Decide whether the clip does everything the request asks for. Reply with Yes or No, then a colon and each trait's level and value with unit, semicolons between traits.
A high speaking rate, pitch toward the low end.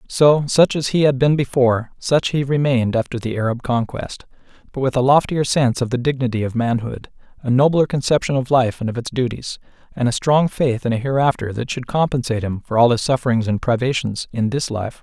Yes: fast, 210 wpm; low, 125 Hz